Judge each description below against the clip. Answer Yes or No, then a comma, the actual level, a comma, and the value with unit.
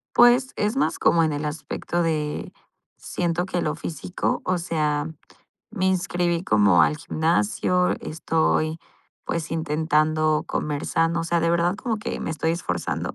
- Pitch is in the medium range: Yes, medium, 165 Hz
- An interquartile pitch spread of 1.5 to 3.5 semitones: Yes, narrow, 2.4 semitones